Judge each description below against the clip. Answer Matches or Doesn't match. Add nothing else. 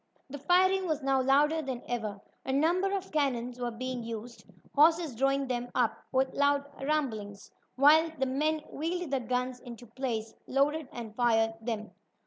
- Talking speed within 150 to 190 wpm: Matches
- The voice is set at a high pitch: Matches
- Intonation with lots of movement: Doesn't match